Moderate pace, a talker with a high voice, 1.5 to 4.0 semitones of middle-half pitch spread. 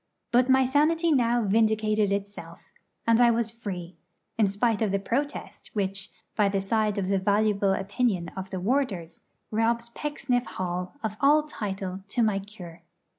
Yes: average, 160 wpm; high, 215 Hz; average, 3.6 semitones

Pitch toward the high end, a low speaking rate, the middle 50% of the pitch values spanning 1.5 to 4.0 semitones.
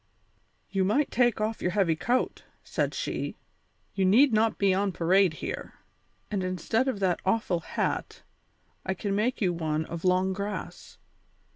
No: high, 195 Hz; average, 155 wpm; average, 3.0 semitones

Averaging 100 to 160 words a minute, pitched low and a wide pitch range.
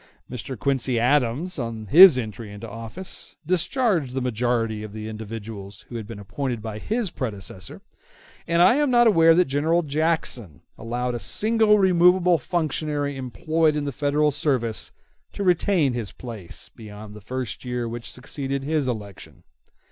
Yes: average, 155 wpm; low, 130 Hz; wide, 6.4 semitones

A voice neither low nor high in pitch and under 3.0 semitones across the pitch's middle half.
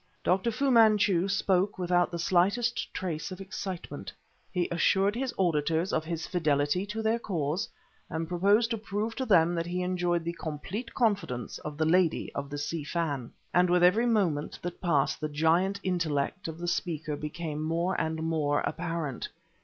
No: medium, 175 Hz; average, 3.5 semitones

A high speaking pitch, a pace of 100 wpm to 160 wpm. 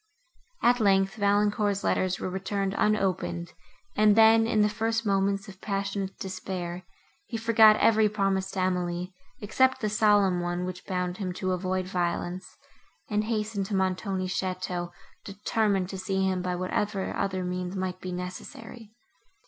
Yes: high, 195 Hz; average, 150 wpm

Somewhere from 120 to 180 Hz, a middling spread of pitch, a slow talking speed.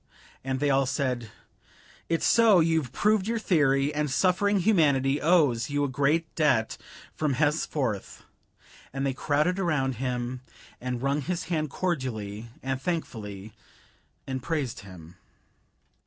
Yes: medium, 140 Hz; average, 4.3 semitones; slow, 130 wpm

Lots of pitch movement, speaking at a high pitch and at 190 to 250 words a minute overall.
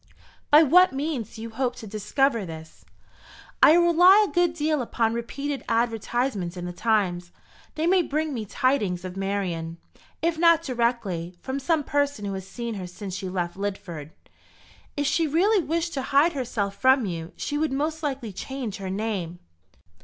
No: wide, 7.3 semitones; high, 240 Hz; average, 170 wpm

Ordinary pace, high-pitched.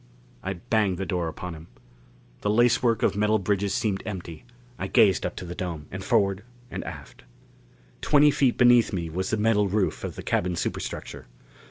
No: average, 180 wpm; low, 100 Hz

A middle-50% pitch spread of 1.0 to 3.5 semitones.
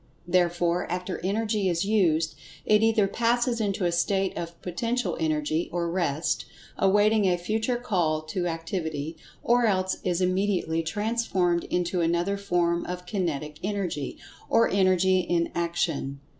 Yes: average, 3.1 semitones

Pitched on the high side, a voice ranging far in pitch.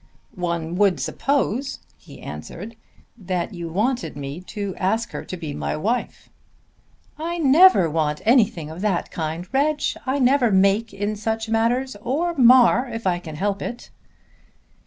Yes: high, 210 Hz; wide, 6.0 semitones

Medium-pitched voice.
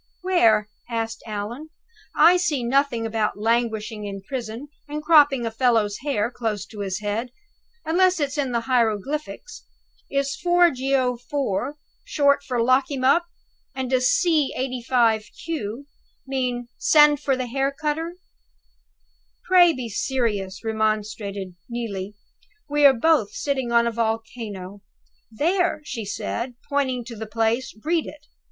No: very high, 250 Hz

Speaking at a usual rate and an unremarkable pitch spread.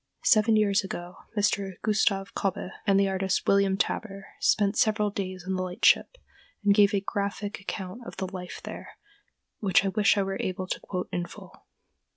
No: average, 180 wpm; narrow, 1.4 semitones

